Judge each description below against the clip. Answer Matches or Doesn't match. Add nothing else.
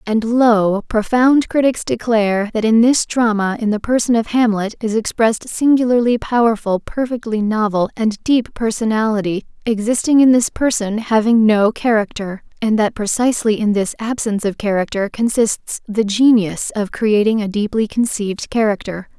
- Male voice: Doesn't match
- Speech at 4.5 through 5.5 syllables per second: Matches